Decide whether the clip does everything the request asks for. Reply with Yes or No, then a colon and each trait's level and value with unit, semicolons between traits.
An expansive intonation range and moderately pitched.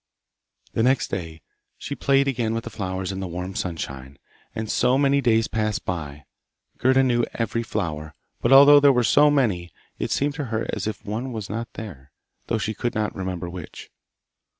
No: wide, 5.7 semitones; low, 110 Hz